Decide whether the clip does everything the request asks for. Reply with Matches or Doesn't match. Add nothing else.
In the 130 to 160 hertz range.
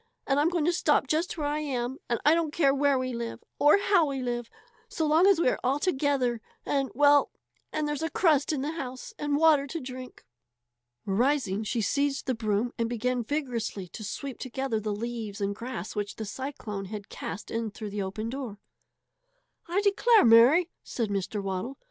Doesn't match